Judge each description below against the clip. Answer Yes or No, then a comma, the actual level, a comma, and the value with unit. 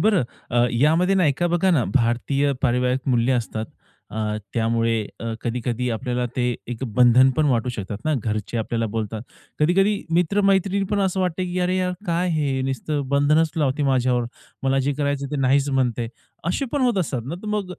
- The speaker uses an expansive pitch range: Yes, wide, 6.2 semitones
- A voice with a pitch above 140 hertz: No, low, 135 Hz